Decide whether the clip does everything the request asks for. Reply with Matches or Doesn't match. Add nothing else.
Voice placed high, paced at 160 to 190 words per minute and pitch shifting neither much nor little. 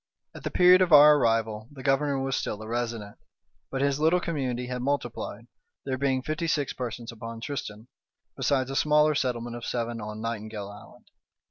Doesn't match